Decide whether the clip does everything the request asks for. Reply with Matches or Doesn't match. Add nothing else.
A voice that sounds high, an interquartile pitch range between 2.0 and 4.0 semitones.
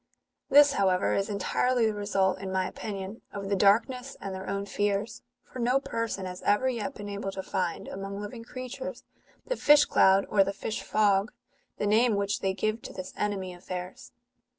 Matches